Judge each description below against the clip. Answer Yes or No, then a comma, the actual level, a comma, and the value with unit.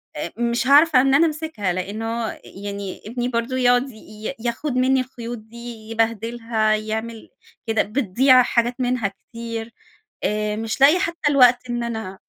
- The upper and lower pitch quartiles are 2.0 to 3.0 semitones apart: Yes, narrow, 2.6 semitones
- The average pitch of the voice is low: No, high, 235 Hz